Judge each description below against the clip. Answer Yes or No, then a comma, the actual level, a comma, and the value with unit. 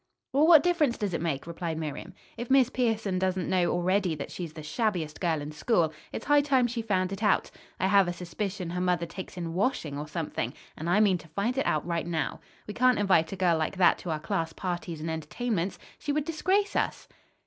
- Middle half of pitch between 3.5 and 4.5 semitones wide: No, average, 5.3 semitones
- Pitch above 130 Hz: Yes, medium, 185 Hz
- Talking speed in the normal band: No, fast, 225 wpm